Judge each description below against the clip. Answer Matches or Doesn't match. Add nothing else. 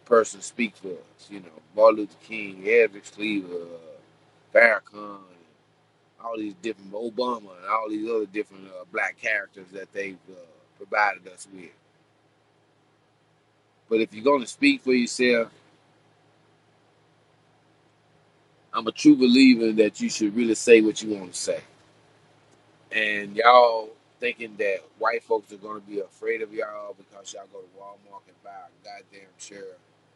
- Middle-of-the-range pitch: Doesn't match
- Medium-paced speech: Matches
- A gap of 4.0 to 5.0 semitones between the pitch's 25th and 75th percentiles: Matches